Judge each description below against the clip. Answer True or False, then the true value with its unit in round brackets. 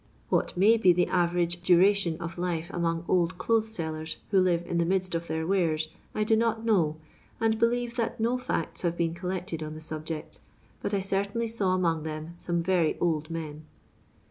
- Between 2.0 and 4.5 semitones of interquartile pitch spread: True (3.4 semitones)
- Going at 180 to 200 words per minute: True (195 wpm)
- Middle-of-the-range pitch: True (175 Hz)